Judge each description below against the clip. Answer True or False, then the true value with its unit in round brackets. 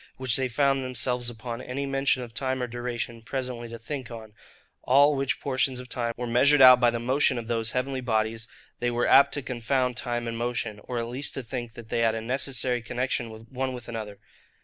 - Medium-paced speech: False (215 wpm)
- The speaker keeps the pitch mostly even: True (2.0 semitones)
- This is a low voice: True (125 Hz)